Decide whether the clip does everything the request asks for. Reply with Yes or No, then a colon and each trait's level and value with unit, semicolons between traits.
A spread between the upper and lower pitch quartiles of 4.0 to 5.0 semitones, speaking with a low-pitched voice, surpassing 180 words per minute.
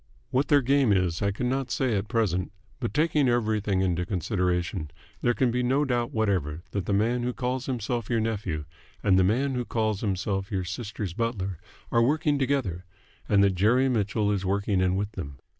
Yes: average, 4.6 semitones; low, 105 Hz; average, 190 wpm